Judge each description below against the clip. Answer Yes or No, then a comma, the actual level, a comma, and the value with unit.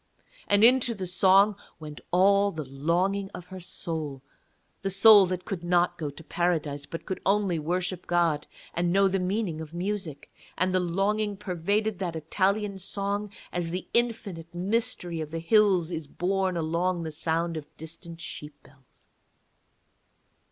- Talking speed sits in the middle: Yes, average, 155 wpm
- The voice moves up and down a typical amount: Yes, average, 3.2 semitones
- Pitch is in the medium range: Yes, medium, 180 Hz